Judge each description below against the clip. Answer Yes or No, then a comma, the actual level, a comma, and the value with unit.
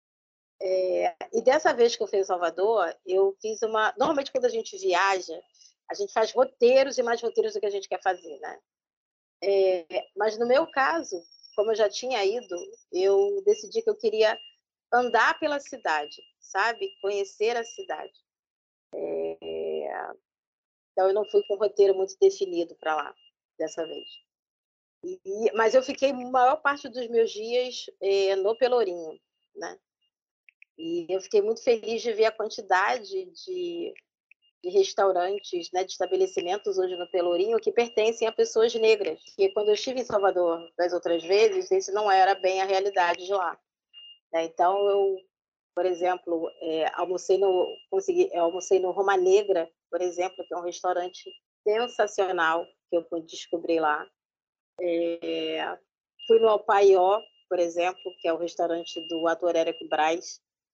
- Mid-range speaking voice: No, high, 205 Hz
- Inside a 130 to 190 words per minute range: Yes, average, 160 wpm